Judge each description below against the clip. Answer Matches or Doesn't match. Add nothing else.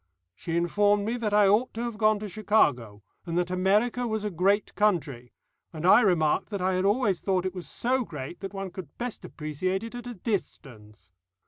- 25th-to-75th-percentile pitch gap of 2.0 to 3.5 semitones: Doesn't match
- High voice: Matches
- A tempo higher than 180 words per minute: Matches